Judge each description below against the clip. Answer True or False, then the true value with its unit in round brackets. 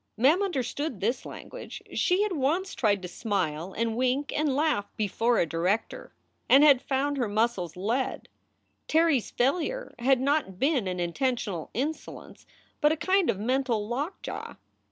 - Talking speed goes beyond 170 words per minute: False (155 wpm)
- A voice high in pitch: True (255 Hz)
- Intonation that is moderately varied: False (6.3 semitones)